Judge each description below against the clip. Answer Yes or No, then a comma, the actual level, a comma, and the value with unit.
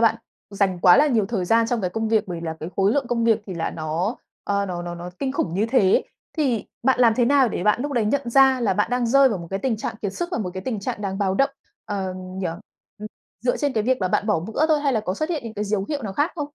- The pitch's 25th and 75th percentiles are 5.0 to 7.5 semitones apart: Yes, average, 5.3 semitones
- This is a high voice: Yes, high, 220 Hz